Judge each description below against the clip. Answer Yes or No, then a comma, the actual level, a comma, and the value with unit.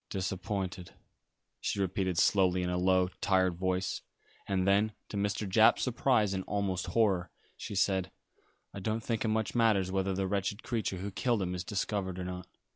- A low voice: Yes, very low, 95 Hz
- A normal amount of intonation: No, narrow, 2.0 semitones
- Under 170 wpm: No, average, 175 wpm